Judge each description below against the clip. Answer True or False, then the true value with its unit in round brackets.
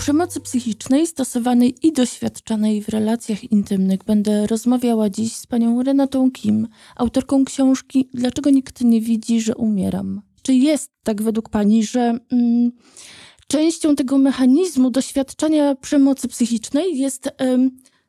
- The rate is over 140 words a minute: False (125 wpm)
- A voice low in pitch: False (250 Hz)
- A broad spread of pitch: False (3.4 semitones)